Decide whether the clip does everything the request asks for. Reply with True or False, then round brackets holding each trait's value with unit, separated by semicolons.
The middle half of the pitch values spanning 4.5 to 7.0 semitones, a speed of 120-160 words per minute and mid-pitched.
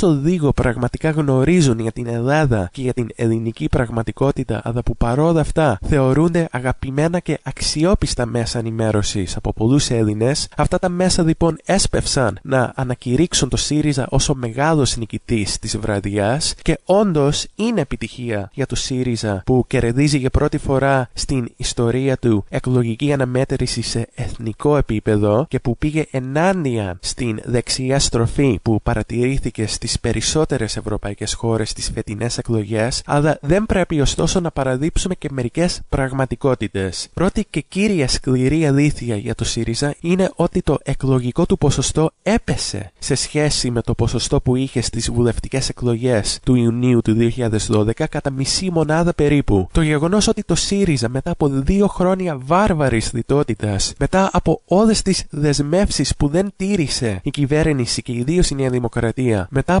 False (4.9 semitones; 145 wpm; 130 Hz)